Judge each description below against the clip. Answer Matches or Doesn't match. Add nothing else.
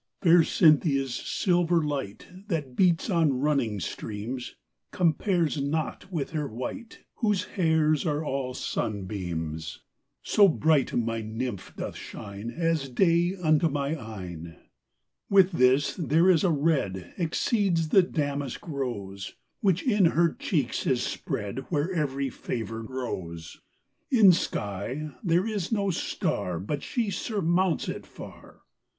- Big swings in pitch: Matches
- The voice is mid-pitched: Matches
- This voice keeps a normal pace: Doesn't match